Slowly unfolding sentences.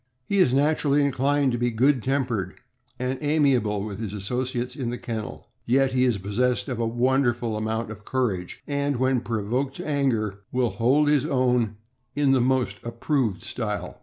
No: average, 175 wpm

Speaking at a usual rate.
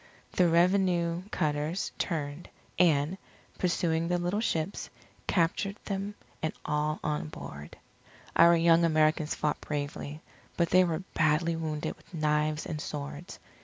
No: slow, 130 wpm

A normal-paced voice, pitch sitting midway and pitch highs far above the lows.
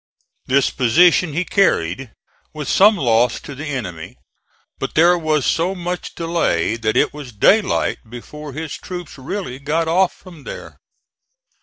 Yes: average, 145 wpm; medium, 150 Hz; wide, 5.8 semitones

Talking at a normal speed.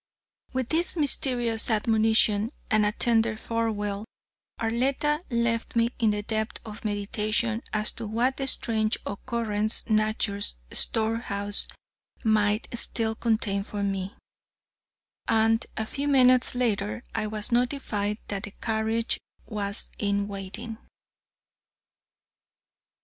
No: slow, 110 wpm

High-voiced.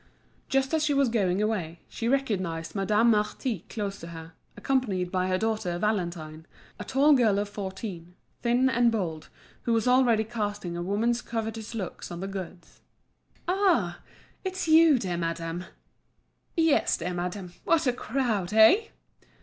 Yes: high, 210 Hz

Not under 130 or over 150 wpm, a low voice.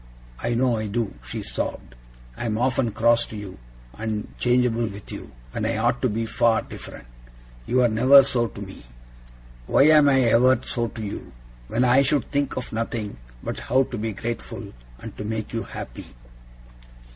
No: average, 180 wpm; low, 115 Hz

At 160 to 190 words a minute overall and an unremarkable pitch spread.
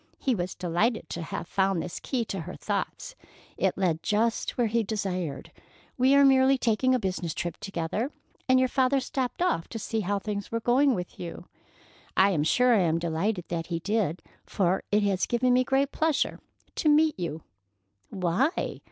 No: average, 185 wpm; wide, 6.3 semitones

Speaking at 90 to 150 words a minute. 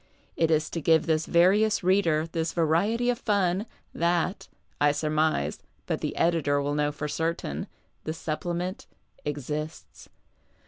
Yes: slow, 135 wpm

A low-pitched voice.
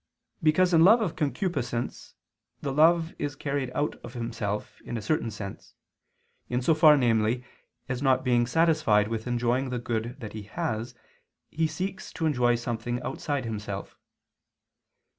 Yes: low, 125 Hz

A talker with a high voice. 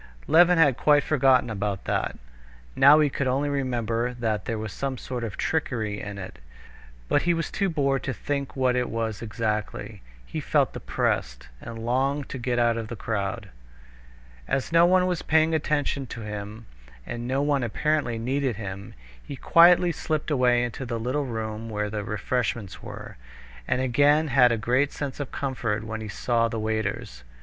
No: low, 125 Hz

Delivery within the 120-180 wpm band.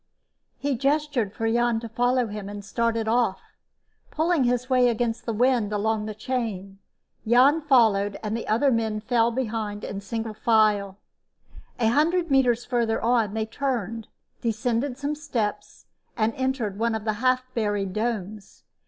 Yes: average, 160 wpm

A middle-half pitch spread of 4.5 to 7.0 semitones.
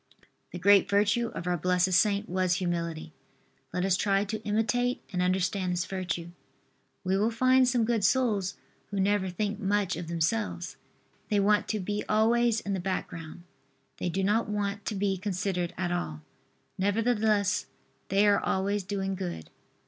No: narrow, 2.6 semitones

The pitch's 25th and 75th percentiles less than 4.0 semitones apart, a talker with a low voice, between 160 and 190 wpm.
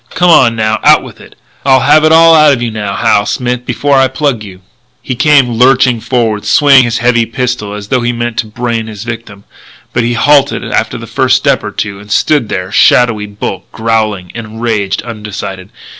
No: average, 3.3 semitones; low, 120 Hz; fast, 205 wpm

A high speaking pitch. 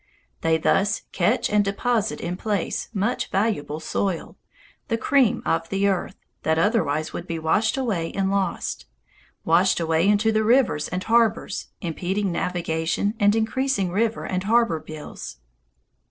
Yes: high, 195 Hz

